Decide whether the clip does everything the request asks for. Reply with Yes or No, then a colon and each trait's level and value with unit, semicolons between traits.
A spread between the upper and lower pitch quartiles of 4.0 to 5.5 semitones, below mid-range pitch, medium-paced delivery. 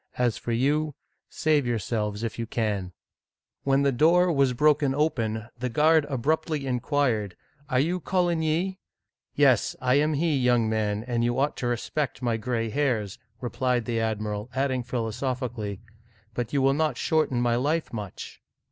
Yes: average, 4.4 semitones; low, 125 Hz; average, 175 wpm